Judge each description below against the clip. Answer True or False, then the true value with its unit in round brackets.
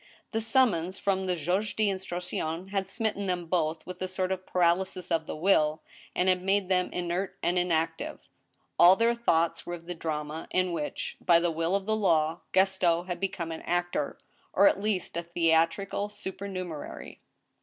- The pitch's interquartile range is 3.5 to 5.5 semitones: False (2.5 semitones)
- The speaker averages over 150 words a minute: True (175 wpm)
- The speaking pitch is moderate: True (180 Hz)